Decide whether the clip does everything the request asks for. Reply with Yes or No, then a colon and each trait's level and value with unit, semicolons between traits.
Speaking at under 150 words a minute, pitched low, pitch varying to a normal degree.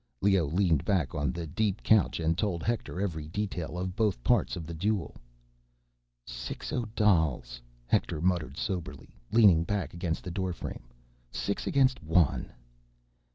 Yes: average, 140 wpm; very low, 90 Hz; average, 4.3 semitones